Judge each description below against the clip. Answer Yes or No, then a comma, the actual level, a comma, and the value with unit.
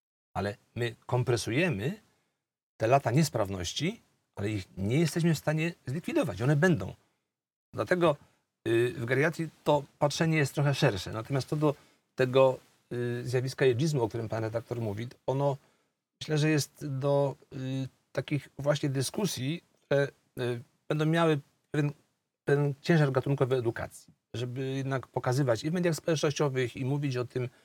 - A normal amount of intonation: Yes, average, 3.6 semitones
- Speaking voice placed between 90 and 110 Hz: No, low, 135 Hz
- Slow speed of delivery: No, average, 130 wpm